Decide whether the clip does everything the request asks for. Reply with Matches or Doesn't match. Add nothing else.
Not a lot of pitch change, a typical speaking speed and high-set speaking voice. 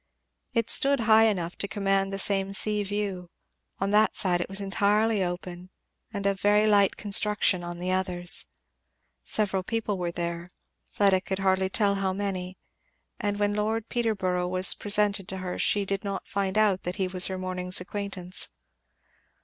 Matches